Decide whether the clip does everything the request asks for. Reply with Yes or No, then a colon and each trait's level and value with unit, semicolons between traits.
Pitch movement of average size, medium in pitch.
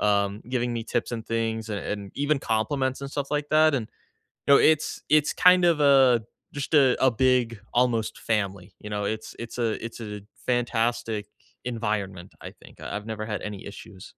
No: average, 3.9 semitones; low, 115 Hz